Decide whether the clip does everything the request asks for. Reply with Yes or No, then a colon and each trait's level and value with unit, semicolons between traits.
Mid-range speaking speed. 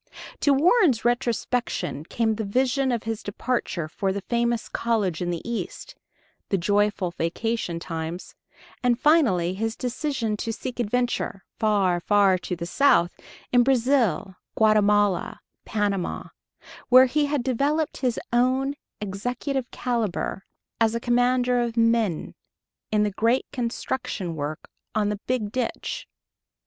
No: slow, 130 wpm